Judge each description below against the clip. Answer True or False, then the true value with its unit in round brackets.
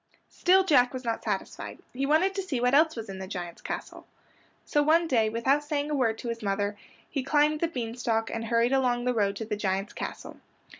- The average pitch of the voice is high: True (245 Hz)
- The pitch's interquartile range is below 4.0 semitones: False (4.9 semitones)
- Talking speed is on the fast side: True (220 wpm)